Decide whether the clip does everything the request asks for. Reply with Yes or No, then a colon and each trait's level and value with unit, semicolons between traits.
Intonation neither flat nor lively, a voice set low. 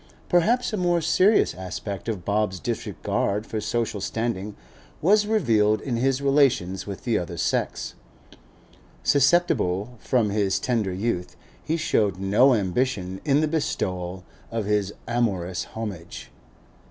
No: wide, 6.1 semitones; low, 110 Hz